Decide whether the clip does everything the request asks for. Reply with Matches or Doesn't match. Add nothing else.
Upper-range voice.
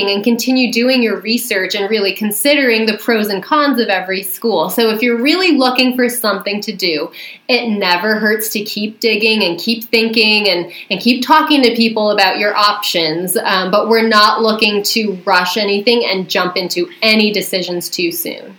Matches